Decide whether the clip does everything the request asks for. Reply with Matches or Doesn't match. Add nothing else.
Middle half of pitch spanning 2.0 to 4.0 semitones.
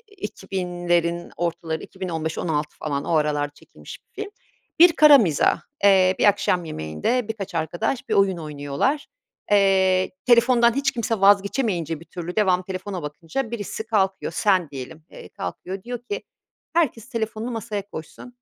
Doesn't match